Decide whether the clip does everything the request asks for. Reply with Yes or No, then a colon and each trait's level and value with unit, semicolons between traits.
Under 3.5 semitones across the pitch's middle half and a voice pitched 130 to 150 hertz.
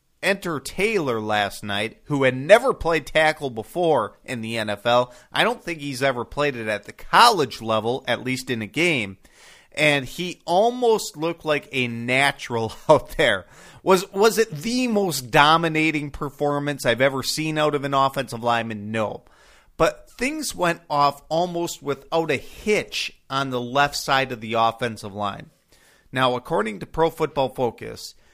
No: average, 5.3 semitones; medium, 140 Hz